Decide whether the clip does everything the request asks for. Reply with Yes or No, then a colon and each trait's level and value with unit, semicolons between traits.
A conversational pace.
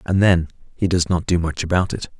No: fast, 245 wpm